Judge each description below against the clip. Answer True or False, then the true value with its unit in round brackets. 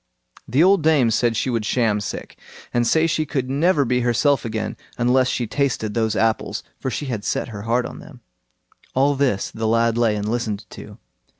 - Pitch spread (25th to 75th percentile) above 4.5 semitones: False (3.6 semitones)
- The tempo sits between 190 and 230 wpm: True (195 wpm)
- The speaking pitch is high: False (120 Hz)